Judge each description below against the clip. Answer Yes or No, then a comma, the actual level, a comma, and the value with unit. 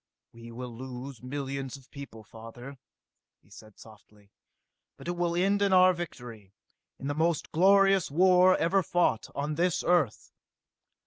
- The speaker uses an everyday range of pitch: No, wide, 6.5 semitones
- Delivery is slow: No, average, 145 wpm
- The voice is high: No, medium, 140 Hz